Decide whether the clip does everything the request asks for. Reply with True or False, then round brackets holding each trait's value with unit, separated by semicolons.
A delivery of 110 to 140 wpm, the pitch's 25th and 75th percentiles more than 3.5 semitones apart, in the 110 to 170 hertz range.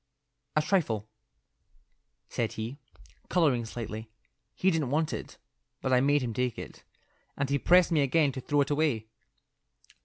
False (150 wpm; 4.4 semitones; 140 Hz)